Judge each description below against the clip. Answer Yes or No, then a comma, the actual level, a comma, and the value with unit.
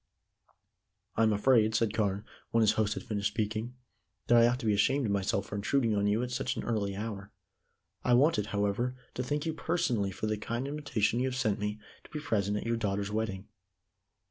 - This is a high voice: No, low, 110 Hz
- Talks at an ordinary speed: No, fast, 210 wpm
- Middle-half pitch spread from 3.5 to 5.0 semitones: No, average, 3.1 semitones